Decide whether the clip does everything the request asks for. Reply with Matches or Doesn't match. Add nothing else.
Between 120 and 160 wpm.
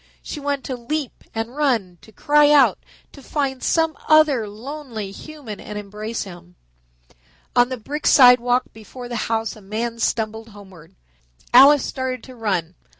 Matches